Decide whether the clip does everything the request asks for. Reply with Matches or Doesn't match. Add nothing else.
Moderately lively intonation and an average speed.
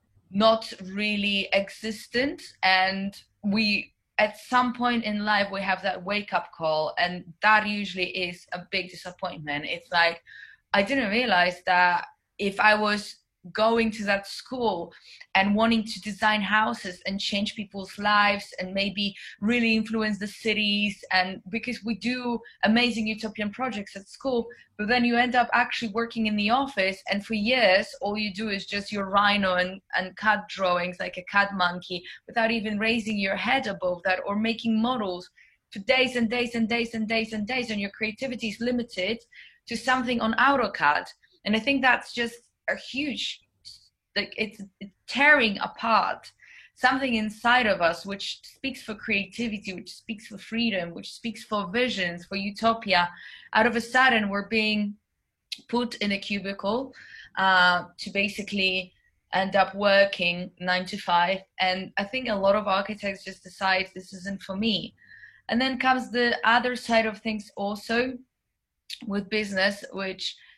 Matches